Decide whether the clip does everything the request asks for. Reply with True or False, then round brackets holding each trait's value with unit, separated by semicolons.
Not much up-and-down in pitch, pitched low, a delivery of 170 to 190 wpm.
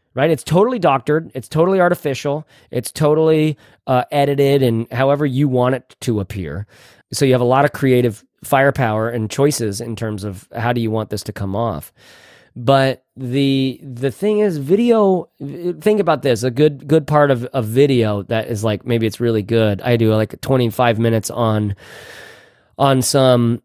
False (4.0 semitones; 130 Hz; 180 wpm)